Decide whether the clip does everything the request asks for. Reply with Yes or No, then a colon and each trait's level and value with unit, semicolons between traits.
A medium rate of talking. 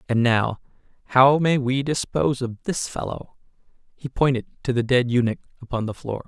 Yes: average, 170 wpm